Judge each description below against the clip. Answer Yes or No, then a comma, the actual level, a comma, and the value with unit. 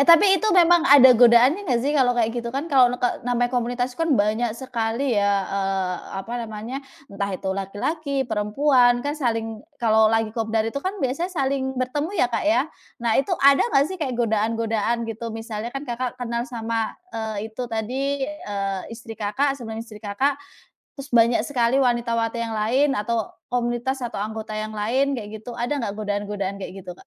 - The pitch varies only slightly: No, average, 3.4 semitones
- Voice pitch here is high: Yes, high, 235 Hz